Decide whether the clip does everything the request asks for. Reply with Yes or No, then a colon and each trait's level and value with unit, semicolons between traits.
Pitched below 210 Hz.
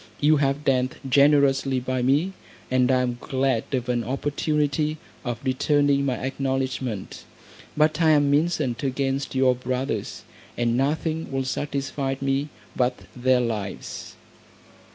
Yes: low, 135 Hz